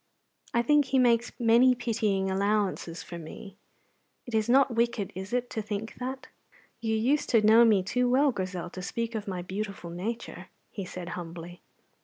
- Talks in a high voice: Yes, high, 220 Hz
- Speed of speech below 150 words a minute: No, average, 175 wpm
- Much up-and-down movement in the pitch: No, average, 4.0 semitones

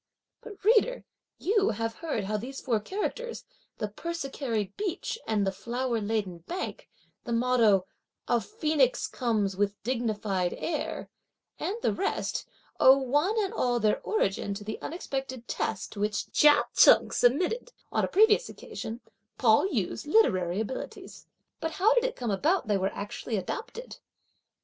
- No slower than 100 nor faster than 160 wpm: Yes, average, 155 wpm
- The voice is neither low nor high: No, high, 245 Hz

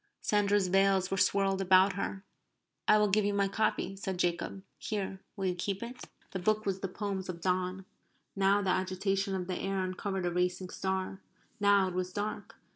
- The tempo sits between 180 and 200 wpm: Yes, average, 190 wpm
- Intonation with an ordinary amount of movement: No, narrow, 1.3 semitones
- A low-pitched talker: No, high, 195 Hz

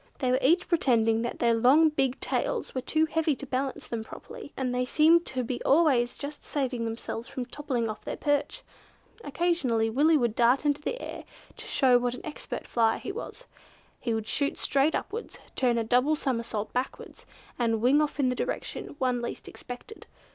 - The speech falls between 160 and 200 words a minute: Yes, average, 190 wpm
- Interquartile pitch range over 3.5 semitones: Yes, average, 3.9 semitones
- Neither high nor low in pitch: No, very high, 255 Hz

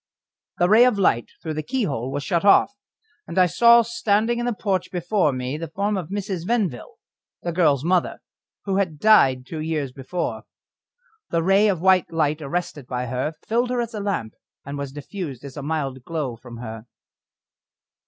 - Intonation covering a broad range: Yes, wide, 6.4 semitones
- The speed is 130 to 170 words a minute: No, average, 180 wpm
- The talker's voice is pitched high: No, medium, 170 Hz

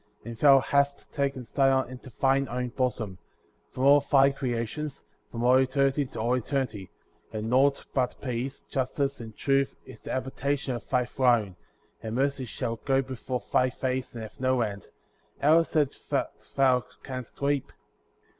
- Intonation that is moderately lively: No, narrow, 2.3 semitones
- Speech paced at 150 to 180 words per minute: Yes, average, 160 wpm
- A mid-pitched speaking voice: No, low, 130 Hz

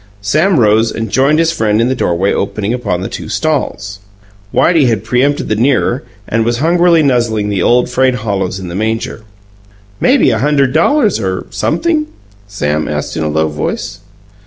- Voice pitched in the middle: No, low, 115 Hz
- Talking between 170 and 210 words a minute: Yes, average, 175 wpm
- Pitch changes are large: Yes, wide, 5.8 semitones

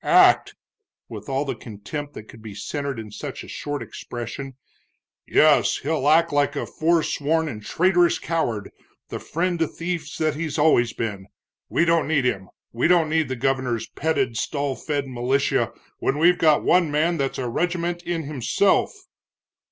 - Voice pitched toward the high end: No, medium, 145 Hz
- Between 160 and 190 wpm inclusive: Yes, average, 165 wpm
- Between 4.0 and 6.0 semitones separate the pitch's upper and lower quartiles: Yes, average, 4.5 semitones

